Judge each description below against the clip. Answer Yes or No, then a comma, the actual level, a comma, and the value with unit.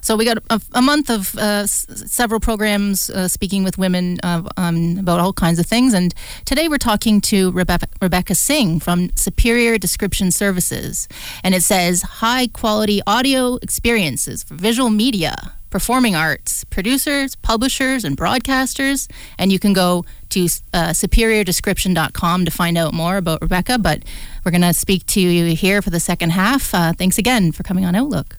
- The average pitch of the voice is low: No, high, 195 Hz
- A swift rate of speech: No, average, 175 wpm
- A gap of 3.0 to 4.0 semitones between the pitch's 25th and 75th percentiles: No, average, 4.4 semitones